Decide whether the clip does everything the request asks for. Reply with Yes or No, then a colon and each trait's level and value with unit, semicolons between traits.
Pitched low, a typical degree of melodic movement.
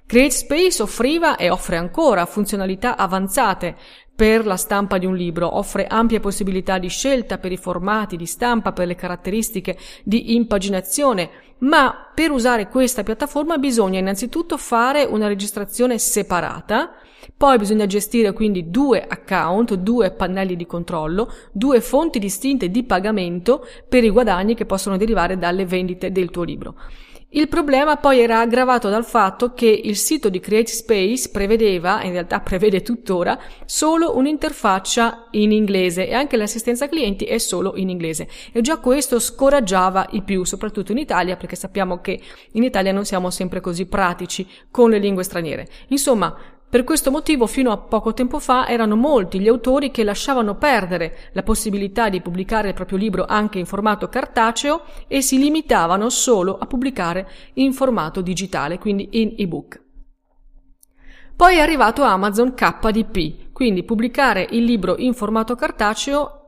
No: high, 215 Hz; average, 5.0 semitones